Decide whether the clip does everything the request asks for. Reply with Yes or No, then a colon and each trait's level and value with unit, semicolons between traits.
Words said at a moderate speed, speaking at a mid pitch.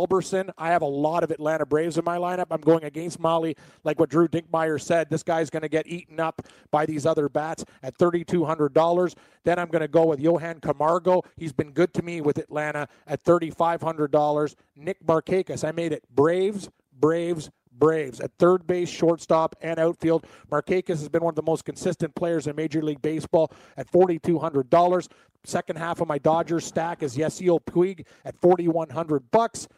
Yes: average, 180 wpm; medium, 165 Hz